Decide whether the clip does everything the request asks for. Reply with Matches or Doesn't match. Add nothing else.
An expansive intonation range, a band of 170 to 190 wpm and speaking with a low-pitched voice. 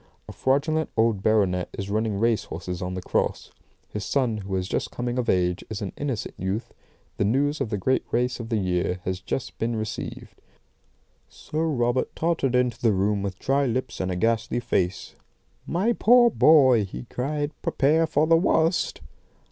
Matches